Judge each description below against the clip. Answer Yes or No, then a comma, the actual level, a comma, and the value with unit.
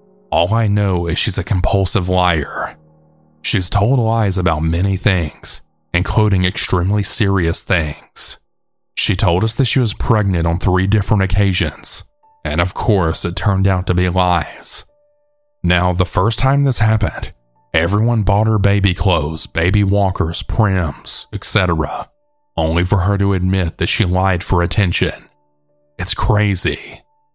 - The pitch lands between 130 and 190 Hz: No, very low, 95 Hz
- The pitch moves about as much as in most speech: Yes, average, 3.6 semitones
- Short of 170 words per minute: Yes, average, 145 wpm